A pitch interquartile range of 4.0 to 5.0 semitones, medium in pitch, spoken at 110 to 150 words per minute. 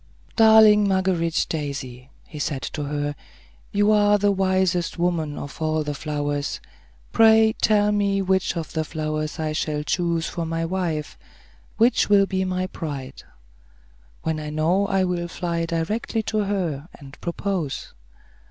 Yes: average, 4.4 semitones; medium, 170 Hz; average, 145 wpm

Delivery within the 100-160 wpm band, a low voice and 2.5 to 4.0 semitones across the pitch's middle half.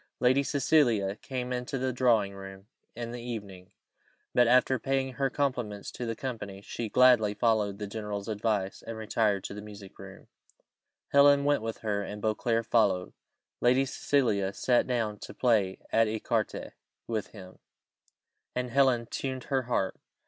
Yes: average, 155 wpm; low, 115 Hz; average, 3.7 semitones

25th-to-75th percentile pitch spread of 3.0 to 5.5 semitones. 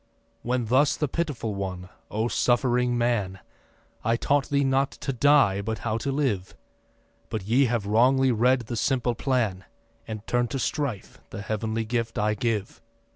Yes: average, 3.5 semitones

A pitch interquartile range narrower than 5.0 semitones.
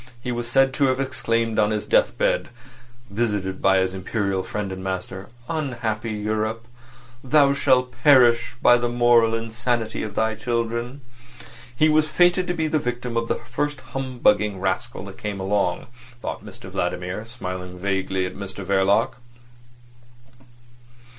Yes: average, 4.3 semitones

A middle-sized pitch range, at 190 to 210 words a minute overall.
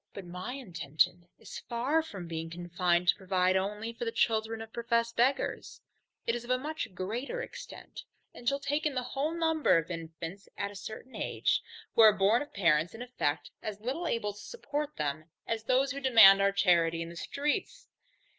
No: wide, 6.4 semitones; average, 195 wpm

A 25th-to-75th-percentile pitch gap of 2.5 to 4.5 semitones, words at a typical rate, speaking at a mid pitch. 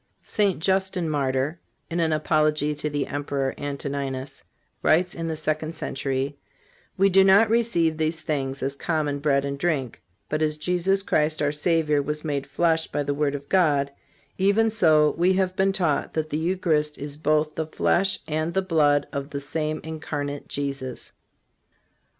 Yes: average, 3.1 semitones; average, 165 wpm; medium, 155 Hz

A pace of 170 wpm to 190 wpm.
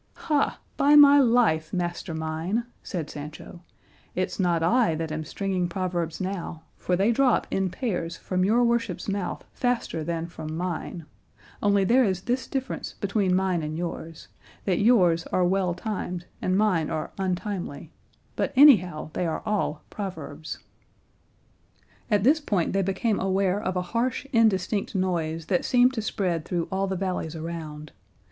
No: average, 155 wpm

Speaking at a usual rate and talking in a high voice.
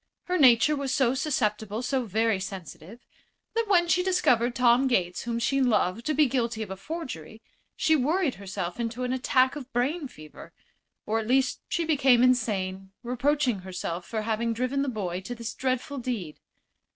Yes: average, 175 wpm; high, 245 Hz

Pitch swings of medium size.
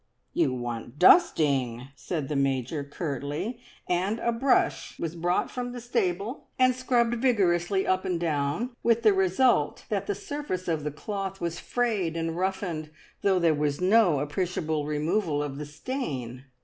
No: wide, 6.4 semitones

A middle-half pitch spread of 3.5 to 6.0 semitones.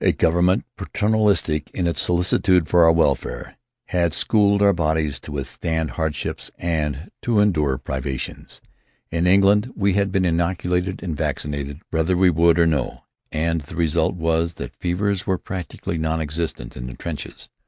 No: average, 3.0 semitones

